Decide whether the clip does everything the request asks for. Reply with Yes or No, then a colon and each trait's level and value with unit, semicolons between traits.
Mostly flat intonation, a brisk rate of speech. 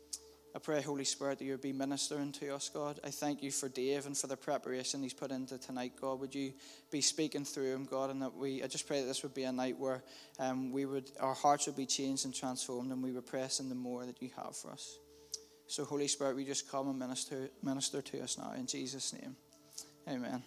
Yes: narrow, 1.6 semitones; fast, 240 wpm